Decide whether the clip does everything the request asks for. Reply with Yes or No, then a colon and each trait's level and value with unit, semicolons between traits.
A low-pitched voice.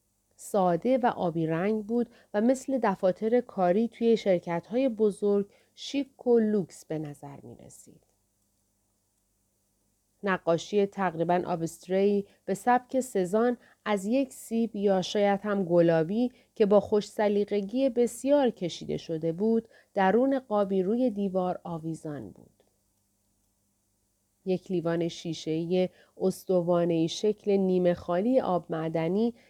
No: high, 190 Hz